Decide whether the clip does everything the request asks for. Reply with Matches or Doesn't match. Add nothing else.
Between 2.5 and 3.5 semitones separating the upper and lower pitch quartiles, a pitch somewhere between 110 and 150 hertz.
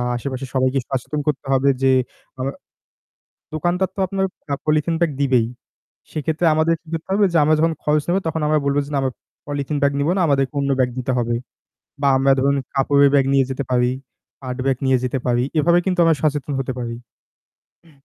Matches